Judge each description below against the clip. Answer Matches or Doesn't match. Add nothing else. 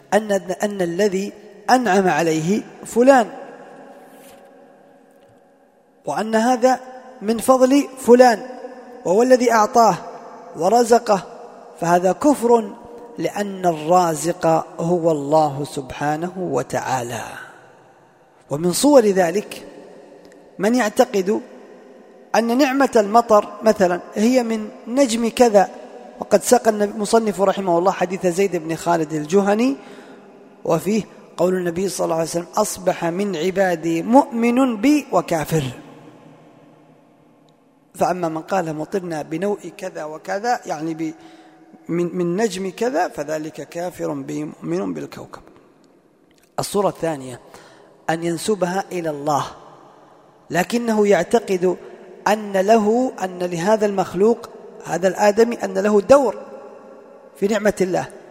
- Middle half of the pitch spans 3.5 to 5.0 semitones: Doesn't match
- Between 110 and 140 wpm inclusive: Doesn't match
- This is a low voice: Doesn't match